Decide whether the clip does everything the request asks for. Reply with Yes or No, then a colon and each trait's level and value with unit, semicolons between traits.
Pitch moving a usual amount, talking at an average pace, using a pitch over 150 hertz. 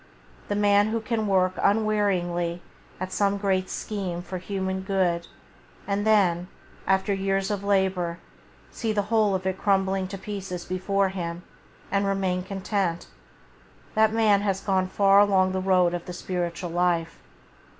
No: narrow, 1.8 semitones; average, 150 wpm; high, 190 Hz